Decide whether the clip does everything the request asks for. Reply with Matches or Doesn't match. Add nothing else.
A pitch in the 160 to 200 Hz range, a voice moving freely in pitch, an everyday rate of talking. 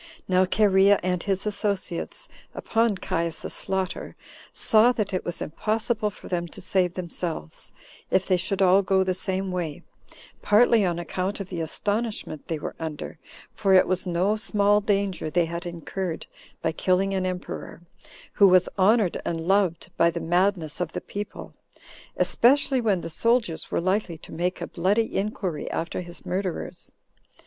Doesn't match